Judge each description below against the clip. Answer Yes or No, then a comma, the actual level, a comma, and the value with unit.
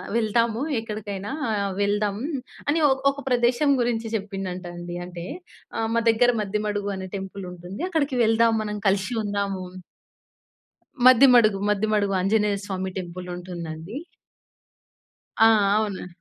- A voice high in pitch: Yes, high, 205 Hz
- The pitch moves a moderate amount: Yes, average, 3.1 semitones